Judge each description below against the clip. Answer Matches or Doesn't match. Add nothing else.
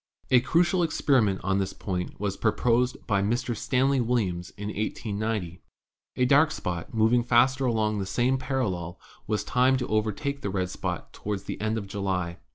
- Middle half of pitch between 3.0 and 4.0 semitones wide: Doesn't match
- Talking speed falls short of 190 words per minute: Matches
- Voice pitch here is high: Doesn't match